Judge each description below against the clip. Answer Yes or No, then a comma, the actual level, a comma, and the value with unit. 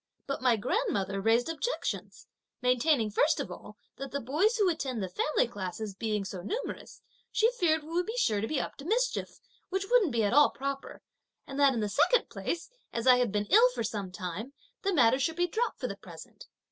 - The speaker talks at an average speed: No, fast, 210 wpm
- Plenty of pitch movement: Yes, wide, 8.2 semitones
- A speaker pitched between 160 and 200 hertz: No, very high, 270 Hz